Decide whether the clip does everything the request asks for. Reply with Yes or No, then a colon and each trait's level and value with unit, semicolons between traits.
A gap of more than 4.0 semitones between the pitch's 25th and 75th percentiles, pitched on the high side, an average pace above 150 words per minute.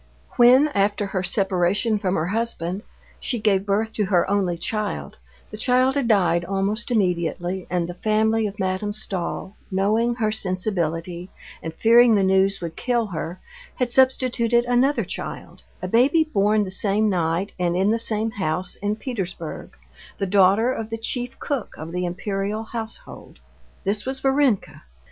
No: average, 3.7 semitones; high, 205 Hz; average, 160 wpm